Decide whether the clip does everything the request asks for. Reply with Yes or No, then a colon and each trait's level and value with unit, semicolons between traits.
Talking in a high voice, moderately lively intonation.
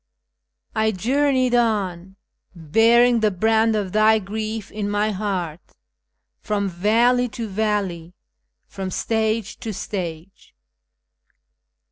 Yes: high, 215 Hz; average, 3.0 semitones